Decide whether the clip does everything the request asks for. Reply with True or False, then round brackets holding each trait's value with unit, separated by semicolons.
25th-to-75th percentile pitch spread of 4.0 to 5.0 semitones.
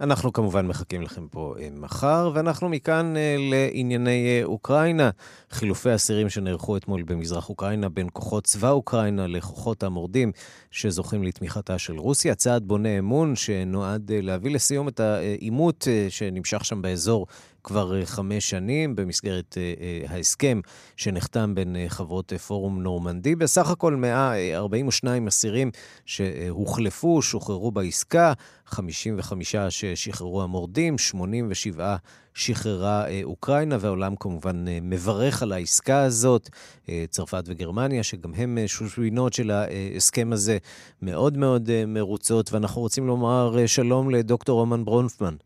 True (4.6 semitones)